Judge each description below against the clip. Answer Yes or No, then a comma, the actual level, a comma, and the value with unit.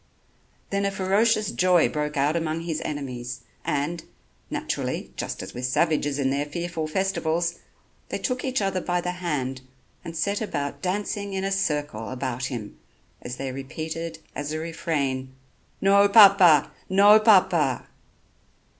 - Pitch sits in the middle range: Yes, medium, 165 Hz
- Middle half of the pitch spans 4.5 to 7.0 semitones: Yes, average, 5.3 semitones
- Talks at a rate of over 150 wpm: No, average, 145 wpm